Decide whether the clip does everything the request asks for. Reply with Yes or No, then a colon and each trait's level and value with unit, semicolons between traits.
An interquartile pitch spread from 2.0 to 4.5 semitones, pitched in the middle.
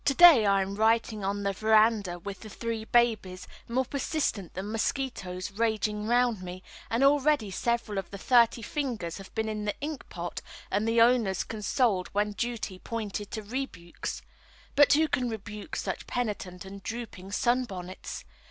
No: average, 3.5 semitones; high, 220 Hz